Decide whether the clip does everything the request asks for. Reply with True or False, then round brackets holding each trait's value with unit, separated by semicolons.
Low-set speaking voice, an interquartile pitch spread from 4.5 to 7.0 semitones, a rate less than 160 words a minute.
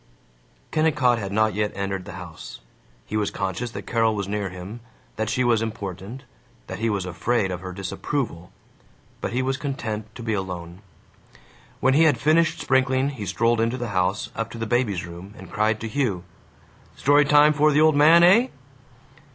False (115 Hz; 5.2 semitones; 185 wpm)